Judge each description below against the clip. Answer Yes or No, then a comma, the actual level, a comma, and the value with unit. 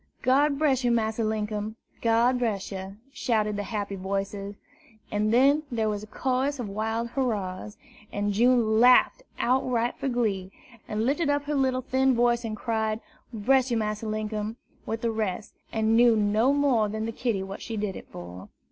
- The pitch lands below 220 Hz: No, high, 225 Hz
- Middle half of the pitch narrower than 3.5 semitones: Yes, average, 3.1 semitones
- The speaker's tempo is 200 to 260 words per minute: No, average, 175 wpm